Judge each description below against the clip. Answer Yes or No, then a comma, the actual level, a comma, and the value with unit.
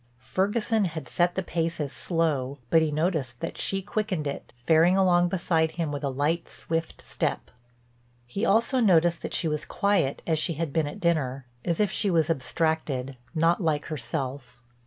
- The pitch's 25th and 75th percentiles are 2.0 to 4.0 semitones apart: Yes, average, 3.4 semitones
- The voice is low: No, medium, 165 Hz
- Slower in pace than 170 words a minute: No, average, 180 wpm